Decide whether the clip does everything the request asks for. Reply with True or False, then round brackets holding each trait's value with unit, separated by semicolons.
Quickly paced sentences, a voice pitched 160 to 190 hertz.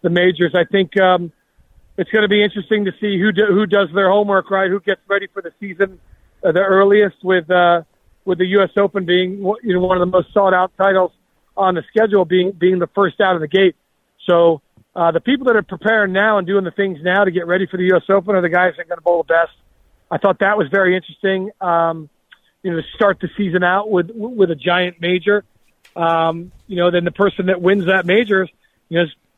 True (240 wpm; 185 Hz)